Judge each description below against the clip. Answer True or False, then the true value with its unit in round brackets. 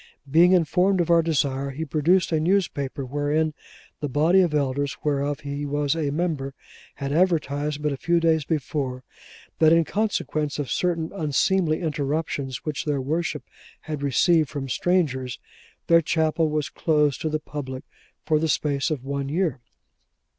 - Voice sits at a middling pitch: True (150 Hz)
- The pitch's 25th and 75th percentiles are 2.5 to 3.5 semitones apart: True (2.8 semitones)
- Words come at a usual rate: True (155 wpm)